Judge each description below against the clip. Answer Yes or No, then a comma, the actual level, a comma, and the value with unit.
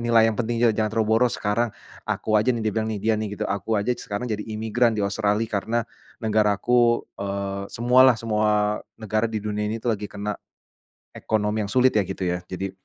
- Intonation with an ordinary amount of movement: No, narrow, 1.8 semitones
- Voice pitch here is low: Yes, low, 110 Hz